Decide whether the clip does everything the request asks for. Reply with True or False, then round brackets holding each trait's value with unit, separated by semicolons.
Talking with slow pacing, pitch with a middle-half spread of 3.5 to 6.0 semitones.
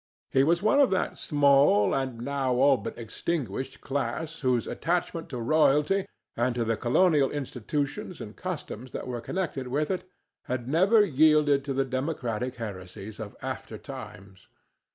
False (155 wpm; 4.8 semitones)